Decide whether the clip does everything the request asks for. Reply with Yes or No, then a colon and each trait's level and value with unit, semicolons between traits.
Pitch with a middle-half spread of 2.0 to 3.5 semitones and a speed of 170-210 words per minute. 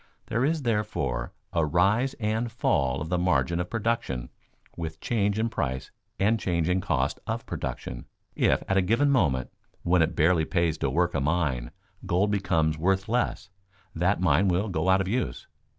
No: average, 5.0 semitones; average, 175 wpm